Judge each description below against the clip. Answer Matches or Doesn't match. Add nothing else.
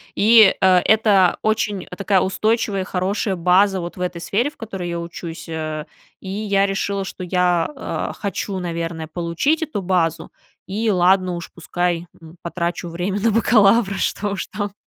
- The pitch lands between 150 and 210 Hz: Matches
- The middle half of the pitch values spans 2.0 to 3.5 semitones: Matches